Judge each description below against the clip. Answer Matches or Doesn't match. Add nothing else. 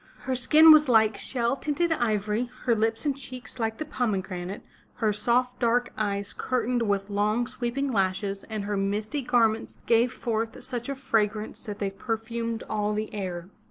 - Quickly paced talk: Doesn't match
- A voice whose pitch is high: Matches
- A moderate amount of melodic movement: Matches